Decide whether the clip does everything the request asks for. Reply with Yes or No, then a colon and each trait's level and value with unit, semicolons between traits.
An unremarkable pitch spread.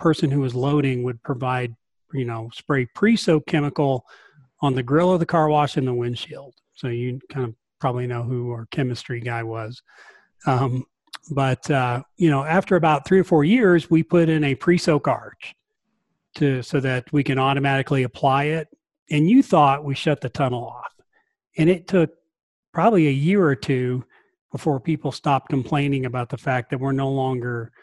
Yes: average, 4.2 semitones